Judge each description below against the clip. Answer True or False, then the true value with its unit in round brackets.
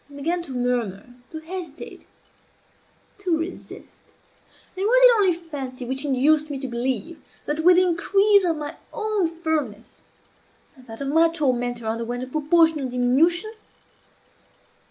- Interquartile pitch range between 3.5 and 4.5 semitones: False (5.3 semitones)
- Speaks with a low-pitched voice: False (305 Hz)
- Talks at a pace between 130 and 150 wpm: True (135 wpm)